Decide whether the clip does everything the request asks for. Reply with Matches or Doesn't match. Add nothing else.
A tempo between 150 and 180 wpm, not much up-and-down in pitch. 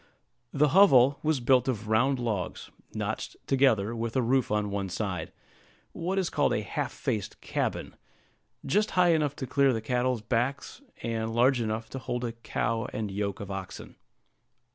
Doesn't match